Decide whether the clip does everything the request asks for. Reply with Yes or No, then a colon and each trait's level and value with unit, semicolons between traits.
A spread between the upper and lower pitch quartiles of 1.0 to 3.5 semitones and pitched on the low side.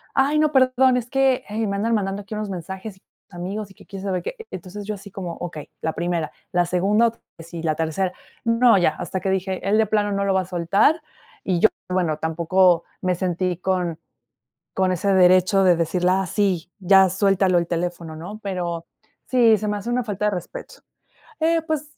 No: average, 3.1 semitones; high, 190 Hz